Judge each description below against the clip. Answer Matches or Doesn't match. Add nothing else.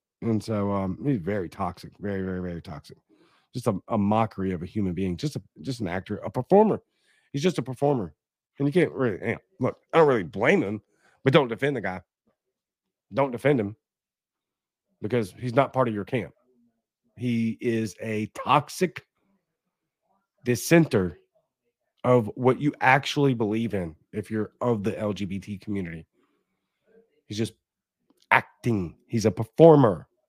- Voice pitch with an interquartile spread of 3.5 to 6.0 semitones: Matches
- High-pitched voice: Doesn't match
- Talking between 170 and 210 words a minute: Doesn't match